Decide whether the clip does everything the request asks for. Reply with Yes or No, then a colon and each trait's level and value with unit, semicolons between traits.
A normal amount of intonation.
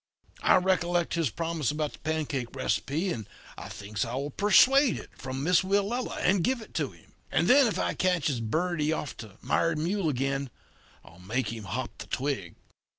No: wide, 6.0 semitones